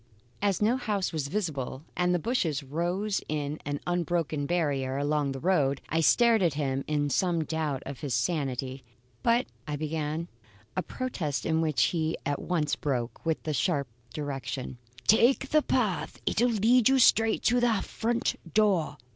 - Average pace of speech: Yes, average, 165 wpm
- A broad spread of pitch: Yes, wide, 6.0 semitones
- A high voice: No, medium, 160 Hz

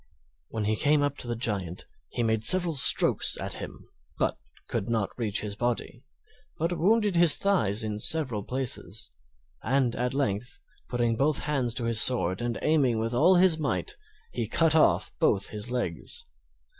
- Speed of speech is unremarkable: Yes, average, 170 wpm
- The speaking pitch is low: Yes, low, 120 Hz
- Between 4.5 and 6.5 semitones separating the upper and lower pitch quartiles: Yes, wide, 5.5 semitones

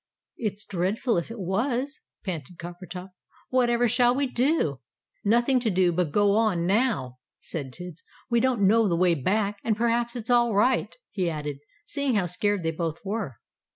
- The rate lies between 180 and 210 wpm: No, average, 170 wpm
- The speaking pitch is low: No, high, 205 Hz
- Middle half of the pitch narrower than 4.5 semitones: No, average, 5.3 semitones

